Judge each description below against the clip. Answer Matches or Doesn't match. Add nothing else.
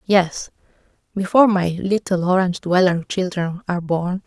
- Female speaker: Matches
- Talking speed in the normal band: Doesn't match